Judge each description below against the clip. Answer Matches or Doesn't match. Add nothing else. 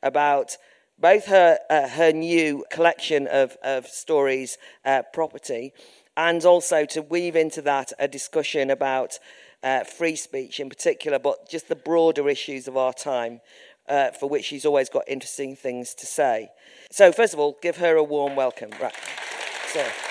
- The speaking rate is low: Doesn't match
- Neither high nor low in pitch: Matches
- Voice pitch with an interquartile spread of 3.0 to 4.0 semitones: Matches